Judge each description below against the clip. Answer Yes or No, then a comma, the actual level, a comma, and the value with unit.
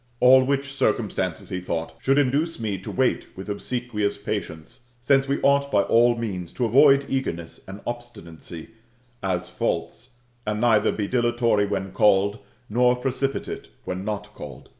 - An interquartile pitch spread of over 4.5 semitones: Yes, average, 5.1 semitones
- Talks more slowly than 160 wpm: Yes, average, 150 wpm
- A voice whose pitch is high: No, low, 115 Hz